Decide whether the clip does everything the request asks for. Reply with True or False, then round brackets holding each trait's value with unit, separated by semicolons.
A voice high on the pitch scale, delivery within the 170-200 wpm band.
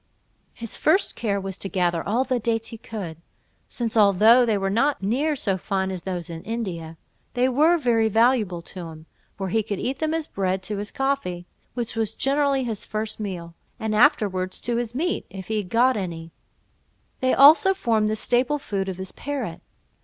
True (220 Hz; 190 wpm)